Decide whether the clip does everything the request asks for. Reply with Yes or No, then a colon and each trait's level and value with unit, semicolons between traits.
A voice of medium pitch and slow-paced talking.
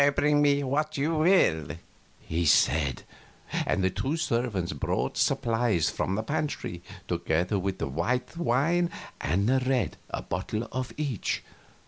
No: low, 115 Hz; slow, 125 wpm